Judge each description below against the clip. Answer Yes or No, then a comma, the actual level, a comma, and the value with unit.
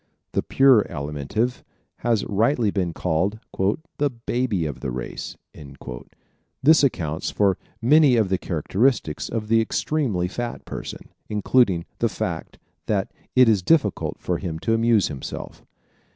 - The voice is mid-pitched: No, low, 105 Hz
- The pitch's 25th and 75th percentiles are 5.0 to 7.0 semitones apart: Yes, wide, 5.4 semitones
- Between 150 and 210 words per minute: No, slow, 135 wpm